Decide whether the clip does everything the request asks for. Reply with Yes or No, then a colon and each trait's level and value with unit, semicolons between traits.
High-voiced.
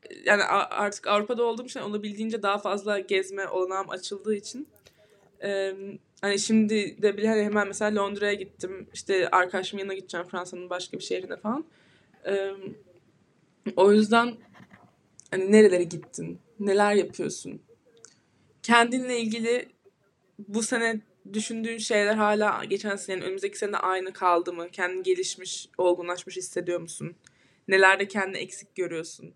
Yes: high, 200 Hz